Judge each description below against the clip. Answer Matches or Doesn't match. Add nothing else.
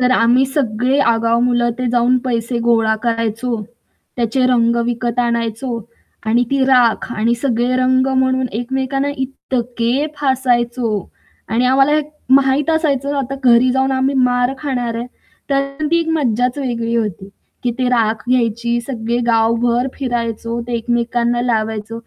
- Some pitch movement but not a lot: Doesn't match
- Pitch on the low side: Doesn't match